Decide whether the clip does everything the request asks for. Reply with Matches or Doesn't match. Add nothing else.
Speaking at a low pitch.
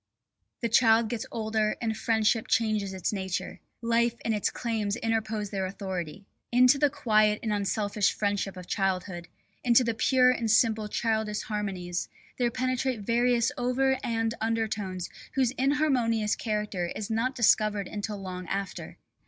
Doesn't match